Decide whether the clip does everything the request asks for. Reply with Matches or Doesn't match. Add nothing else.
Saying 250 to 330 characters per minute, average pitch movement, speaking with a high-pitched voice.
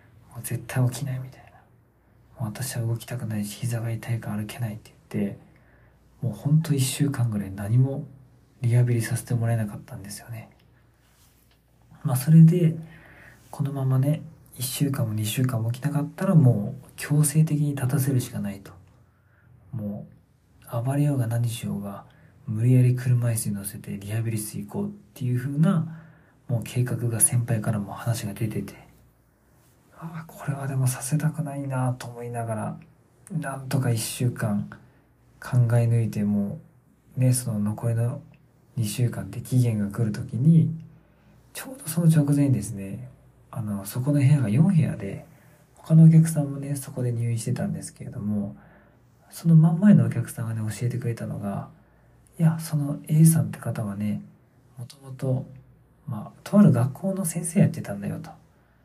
Doesn't match